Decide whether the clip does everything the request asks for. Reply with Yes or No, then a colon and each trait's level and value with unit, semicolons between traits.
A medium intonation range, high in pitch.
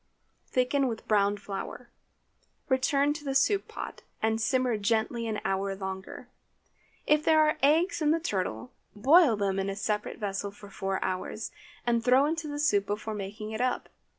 No: wide, 5.7 semitones; high, 225 Hz